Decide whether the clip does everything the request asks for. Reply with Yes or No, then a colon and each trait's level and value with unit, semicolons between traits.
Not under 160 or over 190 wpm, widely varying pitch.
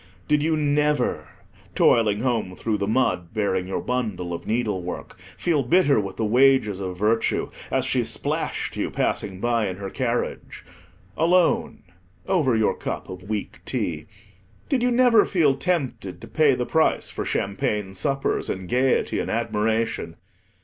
No: average, 150 wpm; wide, 6.3 semitones